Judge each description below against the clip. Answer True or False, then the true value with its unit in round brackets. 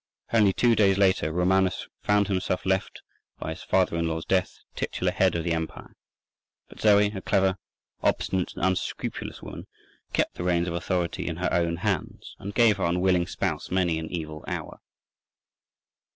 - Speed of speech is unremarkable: True (165 wpm)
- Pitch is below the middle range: True (90 Hz)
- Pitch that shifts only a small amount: True (2.3 semitones)